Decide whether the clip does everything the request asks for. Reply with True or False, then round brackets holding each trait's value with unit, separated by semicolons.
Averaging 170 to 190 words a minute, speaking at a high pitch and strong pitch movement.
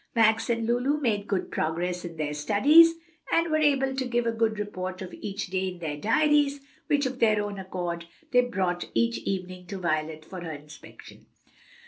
True (185 wpm; 200 Hz; 5.8 semitones)